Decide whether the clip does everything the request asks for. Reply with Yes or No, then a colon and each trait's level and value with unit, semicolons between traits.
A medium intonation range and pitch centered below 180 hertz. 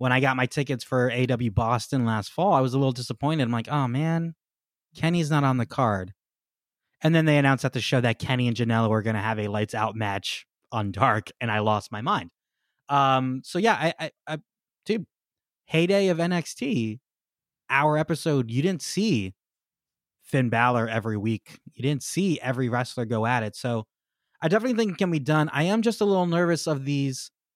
No: wide, 5.7 semitones; low, 135 Hz